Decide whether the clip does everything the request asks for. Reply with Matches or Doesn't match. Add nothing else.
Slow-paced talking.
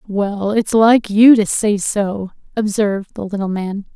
Doesn't match